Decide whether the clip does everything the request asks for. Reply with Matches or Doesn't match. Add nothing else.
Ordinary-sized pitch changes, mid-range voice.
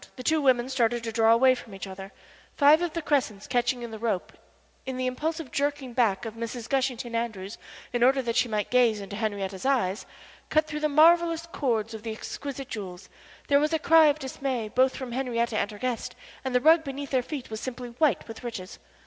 Doesn't match